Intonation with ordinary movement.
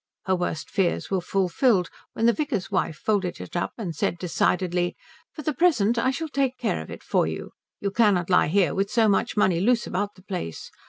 Yes: average, 4.7 semitones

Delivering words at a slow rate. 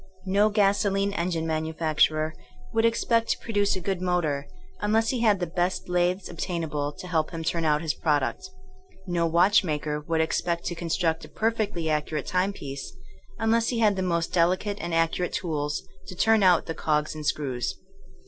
No: average, 175 wpm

